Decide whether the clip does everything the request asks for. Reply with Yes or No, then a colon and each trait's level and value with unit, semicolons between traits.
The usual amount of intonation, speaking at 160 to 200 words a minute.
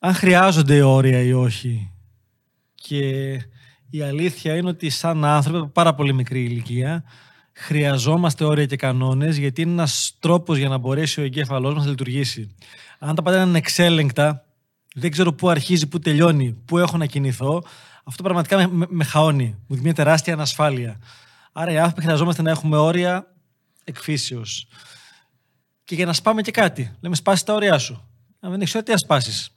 Yes: average, 4.5 semitones; average, 165 wpm